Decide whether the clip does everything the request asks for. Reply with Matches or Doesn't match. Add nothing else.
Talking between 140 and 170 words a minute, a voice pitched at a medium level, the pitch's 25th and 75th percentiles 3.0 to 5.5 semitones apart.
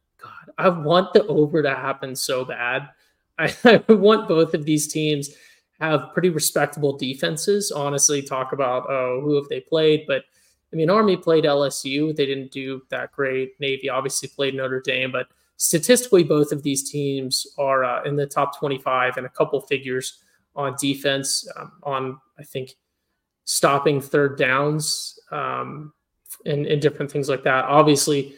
Doesn't match